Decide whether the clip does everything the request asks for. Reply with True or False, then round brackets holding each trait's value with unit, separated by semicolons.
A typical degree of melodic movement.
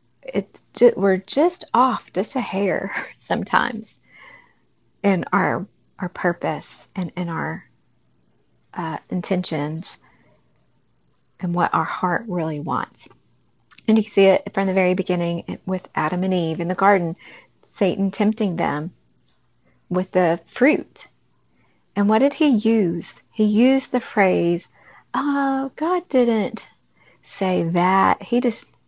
True (4.5 semitones)